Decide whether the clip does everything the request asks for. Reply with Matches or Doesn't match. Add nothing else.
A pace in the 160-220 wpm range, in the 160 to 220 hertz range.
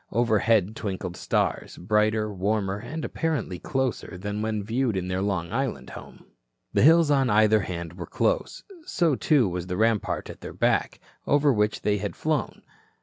Doesn't match